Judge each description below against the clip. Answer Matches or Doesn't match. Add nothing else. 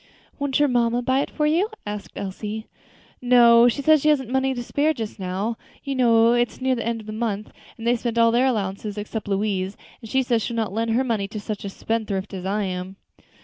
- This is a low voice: Doesn't match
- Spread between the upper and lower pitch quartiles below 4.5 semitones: Matches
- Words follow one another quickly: Matches